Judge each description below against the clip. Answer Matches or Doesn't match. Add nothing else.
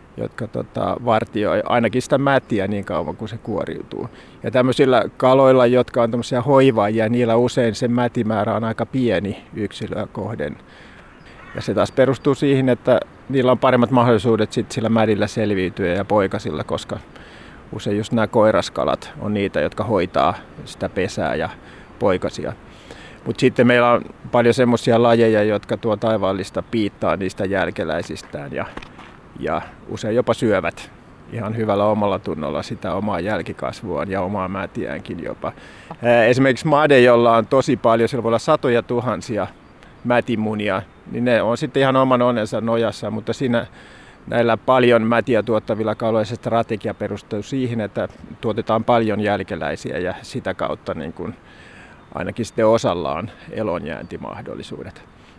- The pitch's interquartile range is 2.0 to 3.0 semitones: Matches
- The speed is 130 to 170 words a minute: Matches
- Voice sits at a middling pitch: Doesn't match